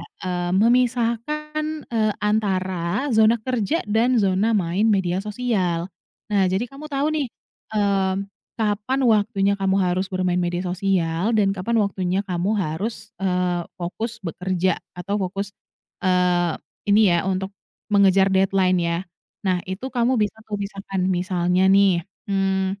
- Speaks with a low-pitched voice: No, high, 195 Hz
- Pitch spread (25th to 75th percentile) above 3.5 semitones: No, average, 3.0 semitones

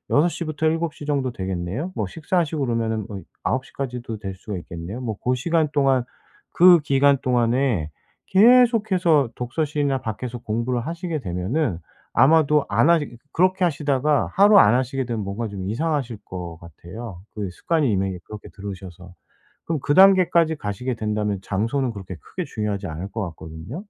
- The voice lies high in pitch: No, low, 125 Hz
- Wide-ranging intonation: Yes, wide, 7.2 semitones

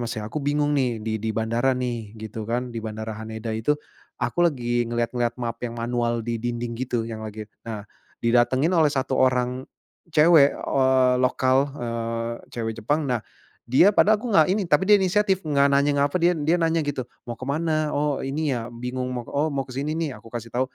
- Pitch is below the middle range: Yes, low, 125 Hz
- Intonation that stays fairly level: No, average, 4.0 semitones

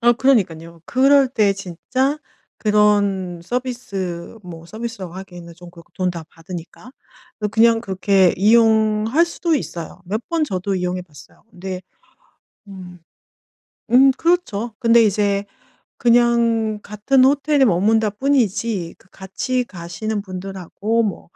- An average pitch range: Yes, average, 4.6 semitones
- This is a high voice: Yes, high, 210 Hz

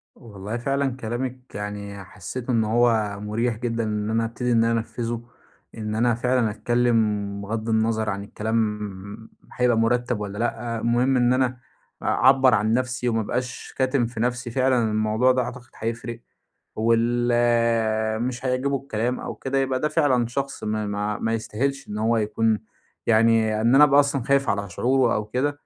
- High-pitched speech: No, low, 115 Hz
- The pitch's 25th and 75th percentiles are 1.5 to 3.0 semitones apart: Yes, narrow, 2.5 semitones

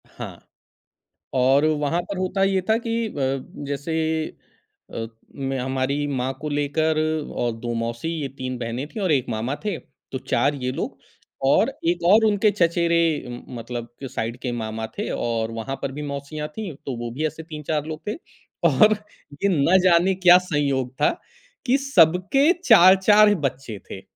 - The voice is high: No, medium, 145 Hz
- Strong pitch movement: Yes, wide, 5.9 semitones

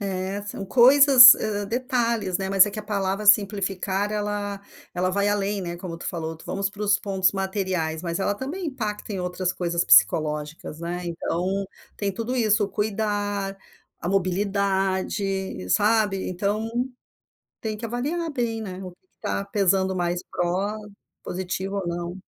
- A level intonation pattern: Yes, narrow, 2.3 semitones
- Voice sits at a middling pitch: No, high, 195 Hz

